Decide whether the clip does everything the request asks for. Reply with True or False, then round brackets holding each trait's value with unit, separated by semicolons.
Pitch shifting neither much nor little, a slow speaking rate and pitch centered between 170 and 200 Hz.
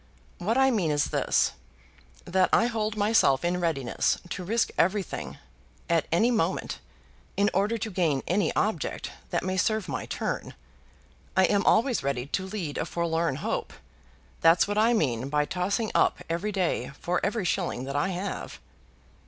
False (4.6 semitones; 160 wpm; 185 Hz)